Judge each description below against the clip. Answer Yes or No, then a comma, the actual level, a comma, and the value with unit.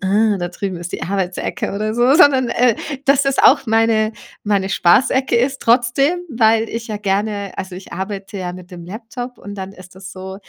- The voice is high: Yes, high, 210 Hz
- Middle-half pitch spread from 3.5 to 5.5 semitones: Yes, average, 4.0 semitones